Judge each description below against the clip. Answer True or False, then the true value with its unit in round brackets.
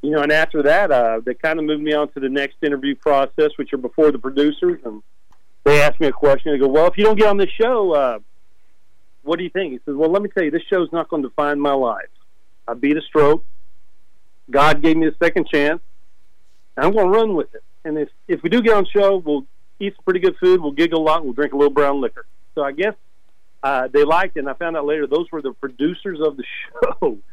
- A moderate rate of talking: False (260 wpm)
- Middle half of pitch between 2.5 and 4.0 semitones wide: False (4.5 semitones)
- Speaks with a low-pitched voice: False (150 Hz)